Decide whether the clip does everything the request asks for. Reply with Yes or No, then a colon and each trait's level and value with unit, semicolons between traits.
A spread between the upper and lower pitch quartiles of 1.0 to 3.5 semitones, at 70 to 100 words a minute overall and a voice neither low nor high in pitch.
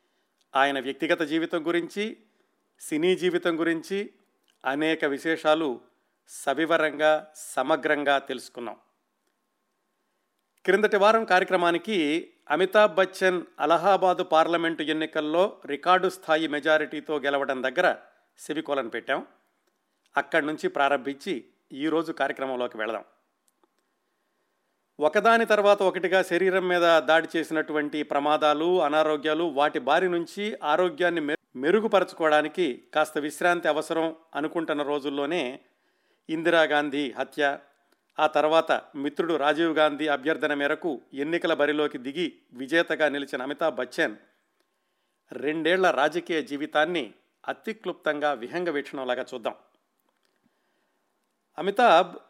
Yes: average, 3.0 semitones; average, 90 wpm; medium, 160 Hz